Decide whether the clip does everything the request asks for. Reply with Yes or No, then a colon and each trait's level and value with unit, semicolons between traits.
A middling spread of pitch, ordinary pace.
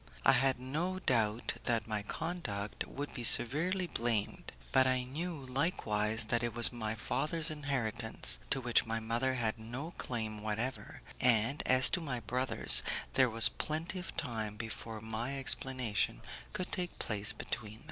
Yes: average, 3.8 semitones; average, 155 wpm